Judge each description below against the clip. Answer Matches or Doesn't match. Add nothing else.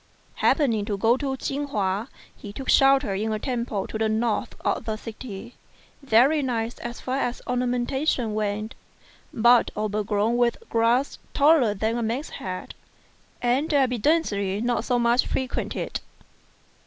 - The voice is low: Doesn't match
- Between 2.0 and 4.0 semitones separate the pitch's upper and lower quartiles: Matches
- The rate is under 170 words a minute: Matches